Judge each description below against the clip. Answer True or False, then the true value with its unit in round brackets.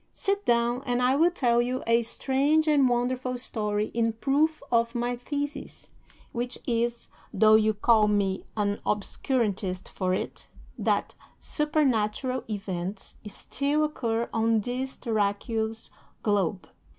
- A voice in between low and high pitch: False (235 Hz)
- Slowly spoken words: True (125 wpm)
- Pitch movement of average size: True (3.4 semitones)